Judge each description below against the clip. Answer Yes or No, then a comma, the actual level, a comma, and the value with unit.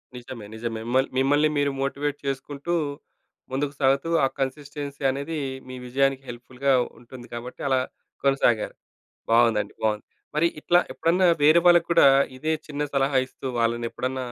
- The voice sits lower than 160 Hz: Yes, low, 135 Hz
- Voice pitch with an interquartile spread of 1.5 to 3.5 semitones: Yes, average, 2.8 semitones